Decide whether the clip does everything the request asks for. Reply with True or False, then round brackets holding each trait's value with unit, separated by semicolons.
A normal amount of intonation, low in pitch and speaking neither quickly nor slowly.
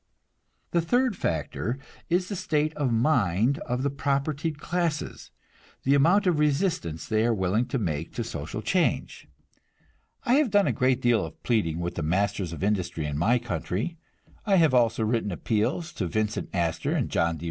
False (8.8 semitones; 120 Hz; 170 wpm)